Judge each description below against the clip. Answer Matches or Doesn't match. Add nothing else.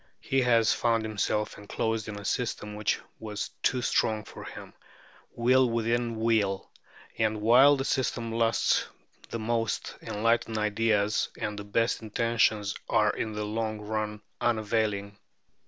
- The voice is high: Doesn't match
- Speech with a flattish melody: Matches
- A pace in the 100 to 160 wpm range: Matches